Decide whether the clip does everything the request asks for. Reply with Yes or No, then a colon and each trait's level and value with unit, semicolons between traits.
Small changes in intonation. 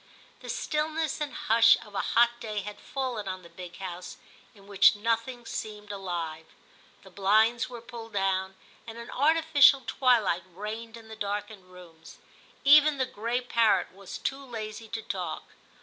No: average, 3.9 semitones